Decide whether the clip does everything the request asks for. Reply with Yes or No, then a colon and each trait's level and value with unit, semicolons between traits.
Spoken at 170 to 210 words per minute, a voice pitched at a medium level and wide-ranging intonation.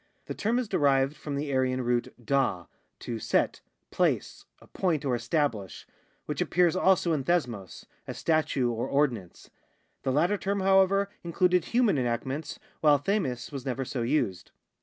No: average, 155 wpm; medium, 145 Hz; wide, 6.2 semitones